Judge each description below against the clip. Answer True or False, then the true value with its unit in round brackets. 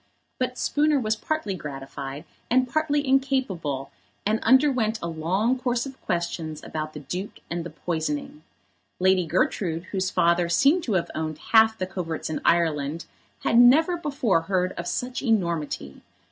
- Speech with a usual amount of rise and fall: False (7.6 semitones)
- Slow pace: False (150 wpm)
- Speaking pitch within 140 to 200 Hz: True (185 Hz)